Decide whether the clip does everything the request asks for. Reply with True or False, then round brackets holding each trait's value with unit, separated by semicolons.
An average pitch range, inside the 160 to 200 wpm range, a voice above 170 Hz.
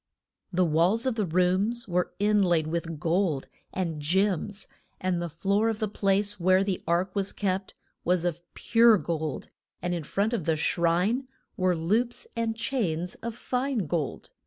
True (3.8 semitones; 165 wpm; 185 Hz)